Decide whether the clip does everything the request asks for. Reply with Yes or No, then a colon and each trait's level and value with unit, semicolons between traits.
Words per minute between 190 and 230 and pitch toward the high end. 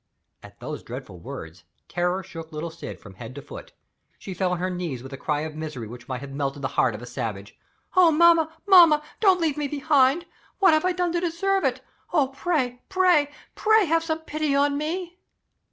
Yes: fast, 205 wpm; very high, 275 Hz